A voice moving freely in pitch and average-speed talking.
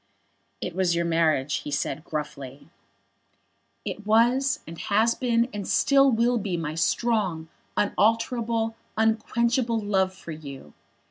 No: wide, 6.2 semitones; slow, 125 wpm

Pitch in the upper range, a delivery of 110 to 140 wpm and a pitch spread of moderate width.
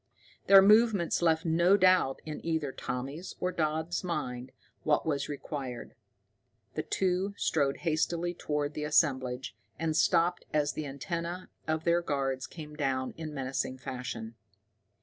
No: medium, 155 Hz; slow, 135 wpm; average, 3.9 semitones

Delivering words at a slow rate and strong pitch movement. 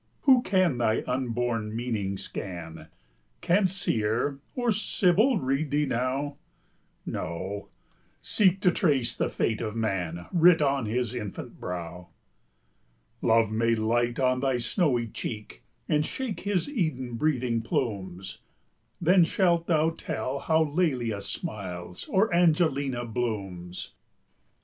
Yes: slow, 120 wpm; wide, 7.0 semitones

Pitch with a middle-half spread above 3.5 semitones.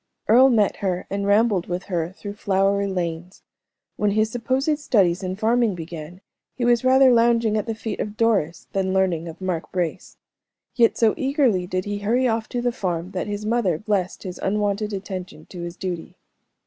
Yes: average, 3.9 semitones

